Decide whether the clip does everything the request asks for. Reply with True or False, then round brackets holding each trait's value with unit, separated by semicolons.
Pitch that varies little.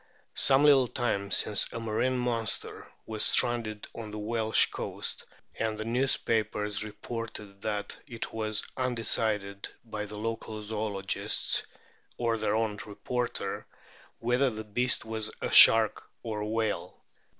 True (1.8 semitones)